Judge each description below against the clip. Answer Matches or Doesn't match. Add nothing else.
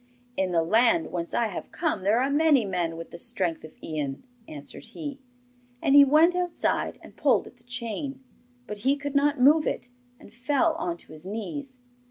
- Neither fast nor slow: Matches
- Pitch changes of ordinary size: Doesn't match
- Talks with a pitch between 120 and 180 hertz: Doesn't match